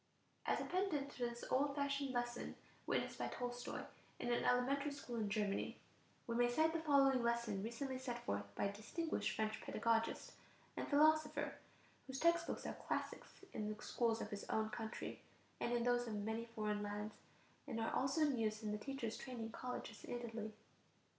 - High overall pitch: Yes, high, 240 Hz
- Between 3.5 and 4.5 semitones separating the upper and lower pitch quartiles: Yes, average, 4.0 semitones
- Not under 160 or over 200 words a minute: Yes, average, 180 wpm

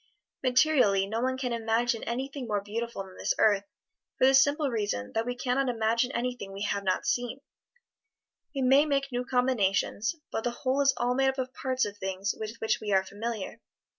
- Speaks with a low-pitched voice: No, high, 240 Hz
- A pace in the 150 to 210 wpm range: Yes, average, 195 wpm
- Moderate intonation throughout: Yes, average, 3.9 semitones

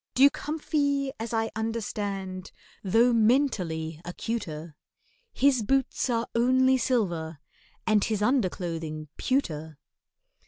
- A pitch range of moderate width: No, wide, 6.8 semitones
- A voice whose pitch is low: No, high, 220 Hz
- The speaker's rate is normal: No, slow, 95 wpm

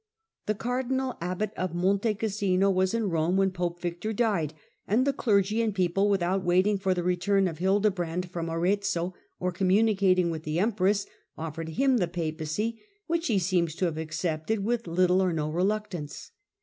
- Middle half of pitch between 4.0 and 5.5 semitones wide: No, average, 3.2 semitones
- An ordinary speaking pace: Yes, average, 175 wpm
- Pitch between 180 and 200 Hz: Yes, medium, 185 Hz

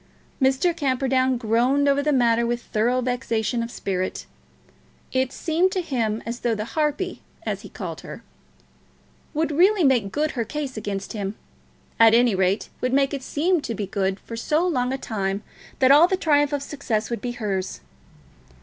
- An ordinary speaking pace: Yes, average, 175 wpm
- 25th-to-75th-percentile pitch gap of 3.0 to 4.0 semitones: No, average, 4.5 semitones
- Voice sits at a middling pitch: No, very high, 255 Hz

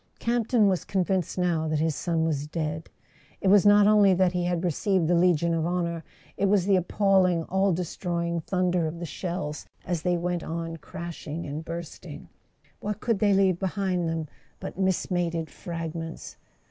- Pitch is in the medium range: Yes, medium, 175 Hz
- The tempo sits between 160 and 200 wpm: Yes, average, 170 wpm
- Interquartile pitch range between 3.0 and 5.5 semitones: No, narrow, 2.5 semitones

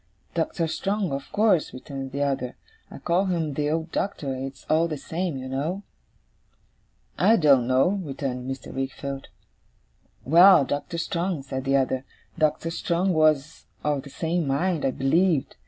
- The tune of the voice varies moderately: Yes, average, 4.0 semitones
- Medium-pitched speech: Yes, medium, 150 Hz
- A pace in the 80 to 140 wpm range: No, average, 155 wpm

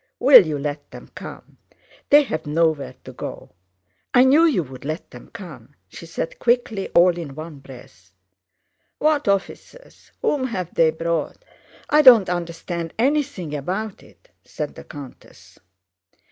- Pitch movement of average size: No, wide, 8.3 semitones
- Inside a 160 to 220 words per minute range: No, average, 140 wpm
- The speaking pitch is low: No, medium, 175 Hz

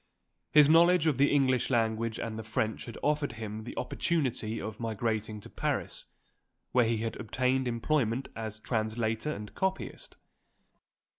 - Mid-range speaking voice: No, low, 115 Hz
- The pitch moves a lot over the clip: No, average, 3.8 semitones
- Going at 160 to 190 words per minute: No, average, 145 wpm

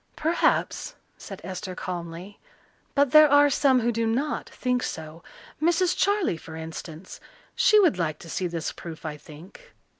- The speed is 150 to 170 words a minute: Yes, average, 155 wpm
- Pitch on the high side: Yes, high, 195 Hz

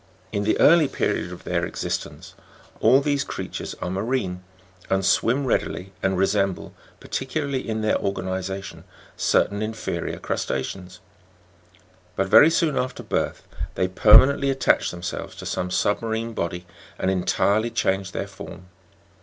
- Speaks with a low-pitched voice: Yes, low, 100 Hz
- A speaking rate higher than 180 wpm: No, slow, 135 wpm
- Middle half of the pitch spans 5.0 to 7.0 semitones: Yes, wide, 5.5 semitones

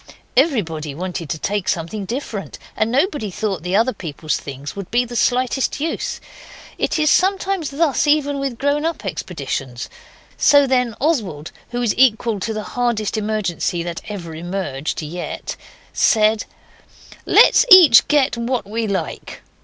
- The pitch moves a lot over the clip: Yes, wide, 7.1 semitones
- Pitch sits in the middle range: No, high, 220 Hz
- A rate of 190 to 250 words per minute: No, average, 145 wpm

